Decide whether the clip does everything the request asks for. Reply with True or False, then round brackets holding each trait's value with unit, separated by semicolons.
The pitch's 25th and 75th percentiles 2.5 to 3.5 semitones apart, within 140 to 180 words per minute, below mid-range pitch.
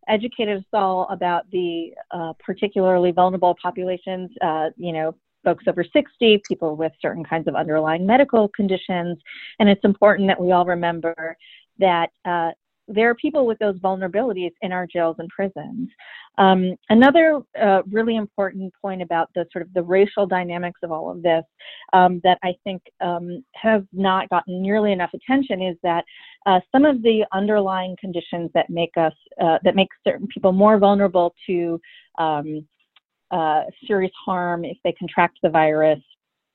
False (2.8 semitones; 165 wpm; 185 Hz)